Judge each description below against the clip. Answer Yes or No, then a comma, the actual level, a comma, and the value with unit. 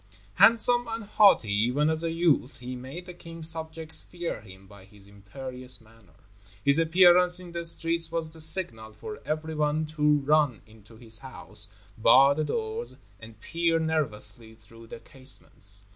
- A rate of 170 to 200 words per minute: No, average, 160 wpm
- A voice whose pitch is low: No, medium, 150 Hz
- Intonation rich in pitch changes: Yes, wide, 6.8 semitones